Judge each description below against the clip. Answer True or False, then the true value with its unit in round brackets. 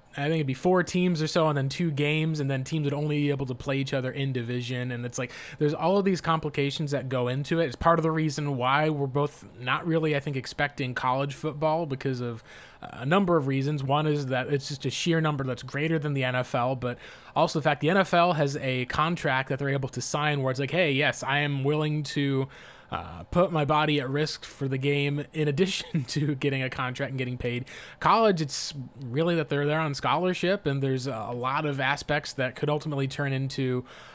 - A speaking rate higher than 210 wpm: True (230 wpm)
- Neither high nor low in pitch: True (145 Hz)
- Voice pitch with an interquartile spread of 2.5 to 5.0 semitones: True (2.8 semitones)